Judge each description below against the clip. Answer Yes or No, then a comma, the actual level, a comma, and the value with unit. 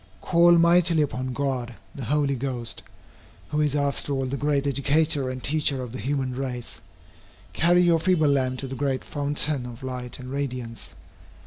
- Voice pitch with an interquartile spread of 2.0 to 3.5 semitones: Yes, average, 2.7 semitones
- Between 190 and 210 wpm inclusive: No, average, 165 wpm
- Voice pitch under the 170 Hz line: Yes, medium, 140 Hz